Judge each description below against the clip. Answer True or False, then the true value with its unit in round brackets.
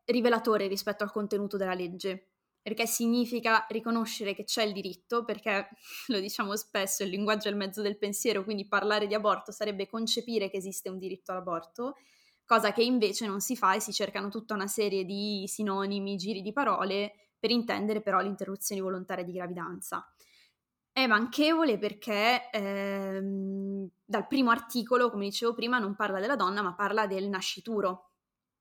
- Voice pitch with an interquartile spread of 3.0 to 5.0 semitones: False (2.4 semitones)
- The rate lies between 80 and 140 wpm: False (165 wpm)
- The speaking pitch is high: True (205 Hz)